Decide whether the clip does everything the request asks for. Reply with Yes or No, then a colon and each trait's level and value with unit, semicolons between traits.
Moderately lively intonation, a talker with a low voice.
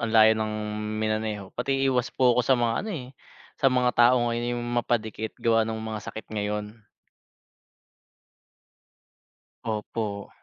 No: narrow, 2.2 semitones; low, 115 Hz